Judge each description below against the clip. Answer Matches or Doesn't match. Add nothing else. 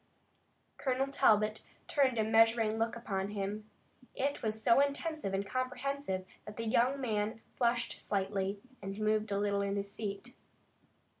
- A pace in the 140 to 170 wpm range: Matches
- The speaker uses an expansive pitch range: Doesn't match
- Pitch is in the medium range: Doesn't match